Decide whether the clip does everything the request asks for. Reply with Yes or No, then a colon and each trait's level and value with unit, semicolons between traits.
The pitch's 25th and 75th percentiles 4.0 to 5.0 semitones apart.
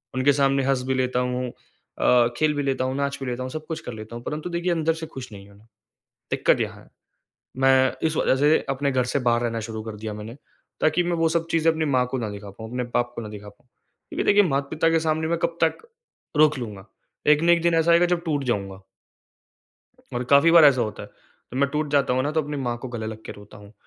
Yes: average, 4.7 semitones